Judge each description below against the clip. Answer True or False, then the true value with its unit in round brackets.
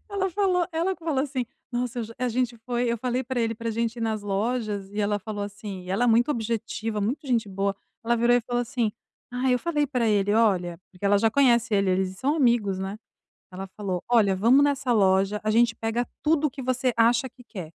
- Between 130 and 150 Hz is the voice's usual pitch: False (230 Hz)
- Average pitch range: True (3.5 semitones)